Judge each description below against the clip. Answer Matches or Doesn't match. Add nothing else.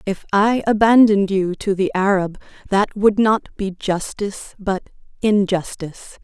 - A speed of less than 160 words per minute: Matches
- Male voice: Doesn't match